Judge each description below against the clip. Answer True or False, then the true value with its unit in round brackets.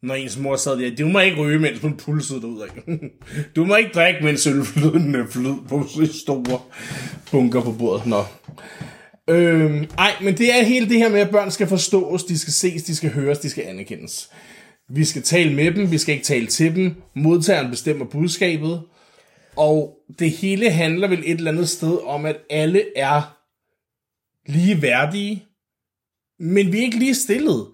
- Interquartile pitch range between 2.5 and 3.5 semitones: False (4.4 semitones)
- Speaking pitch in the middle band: True (155 Hz)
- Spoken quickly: False (175 wpm)